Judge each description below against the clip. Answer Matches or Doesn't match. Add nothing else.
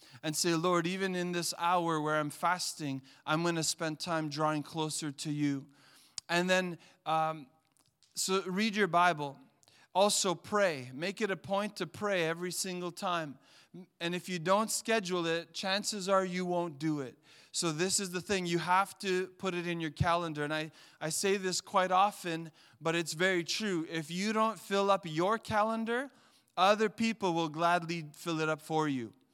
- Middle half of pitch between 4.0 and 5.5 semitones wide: Doesn't match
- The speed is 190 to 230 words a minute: Doesn't match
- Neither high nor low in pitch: Matches